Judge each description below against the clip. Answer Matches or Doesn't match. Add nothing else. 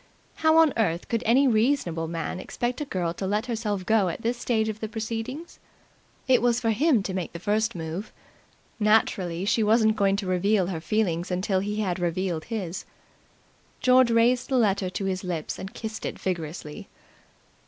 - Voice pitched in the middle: Doesn't match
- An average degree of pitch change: Matches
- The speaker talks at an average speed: Matches